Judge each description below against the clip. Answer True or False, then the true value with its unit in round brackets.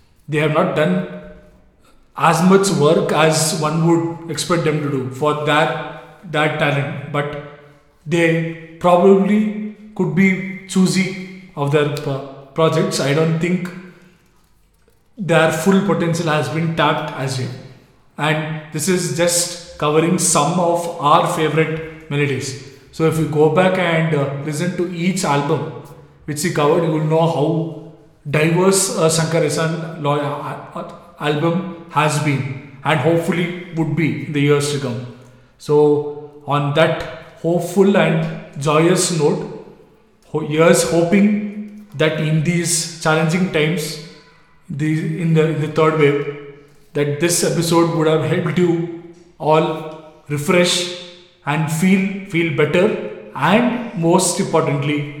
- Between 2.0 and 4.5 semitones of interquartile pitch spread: True (2.5 semitones)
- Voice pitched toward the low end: False (160 Hz)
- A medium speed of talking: False (130 wpm)